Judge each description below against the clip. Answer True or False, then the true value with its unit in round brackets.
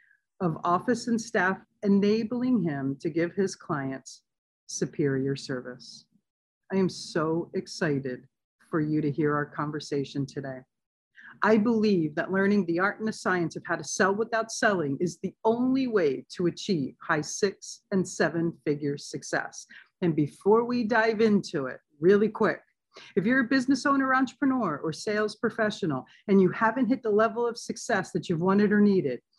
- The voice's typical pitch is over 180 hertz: True (190 Hz)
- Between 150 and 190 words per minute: True (165 wpm)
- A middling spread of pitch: False (6.0 semitones)